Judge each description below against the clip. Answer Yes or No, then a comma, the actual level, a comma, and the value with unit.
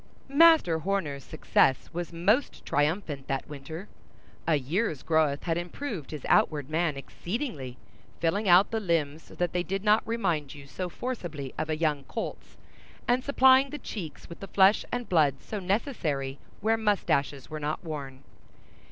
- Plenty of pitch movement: Yes, wide, 5.9 semitones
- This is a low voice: No, medium, 170 Hz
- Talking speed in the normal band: Yes, average, 160 wpm